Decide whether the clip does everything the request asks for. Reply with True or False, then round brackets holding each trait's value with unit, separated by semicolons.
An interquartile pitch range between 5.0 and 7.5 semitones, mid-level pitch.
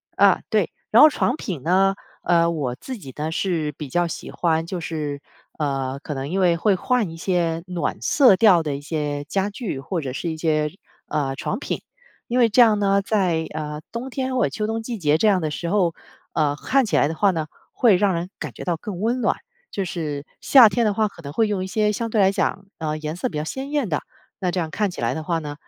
True (5.3 semitones; 175 Hz)